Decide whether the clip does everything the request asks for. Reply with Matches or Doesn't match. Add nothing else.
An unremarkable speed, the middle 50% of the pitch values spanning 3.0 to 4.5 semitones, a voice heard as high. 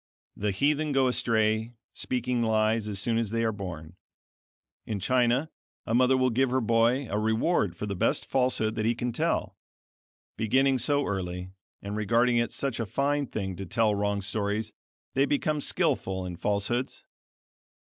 Doesn't match